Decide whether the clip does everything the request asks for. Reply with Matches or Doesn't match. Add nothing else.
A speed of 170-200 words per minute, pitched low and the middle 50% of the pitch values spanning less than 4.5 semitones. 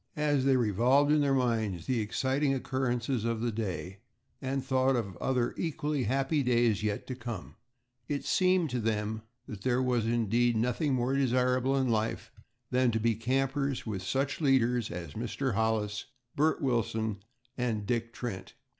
Doesn't match